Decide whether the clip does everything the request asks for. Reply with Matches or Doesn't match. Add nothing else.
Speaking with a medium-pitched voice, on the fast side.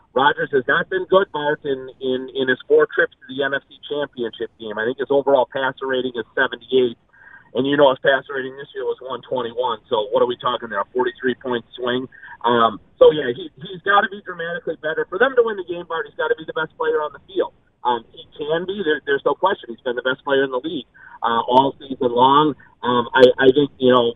Matches